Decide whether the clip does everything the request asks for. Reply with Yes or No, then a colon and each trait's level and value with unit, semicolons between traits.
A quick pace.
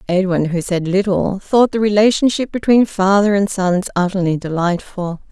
No: average, 145 wpm